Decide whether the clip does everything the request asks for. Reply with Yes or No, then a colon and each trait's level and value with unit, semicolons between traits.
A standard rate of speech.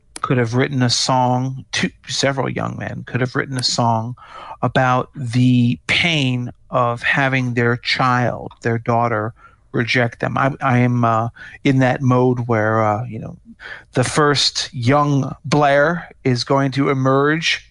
Yes: average, 150 wpm